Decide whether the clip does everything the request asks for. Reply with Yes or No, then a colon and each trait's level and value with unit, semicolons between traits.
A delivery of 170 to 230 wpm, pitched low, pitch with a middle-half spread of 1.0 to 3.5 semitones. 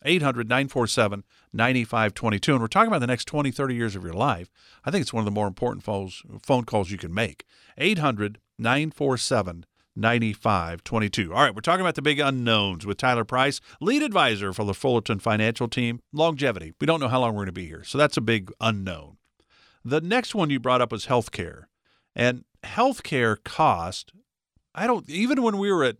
No: average, 185 wpm; low, 120 Hz; average, 5.1 semitones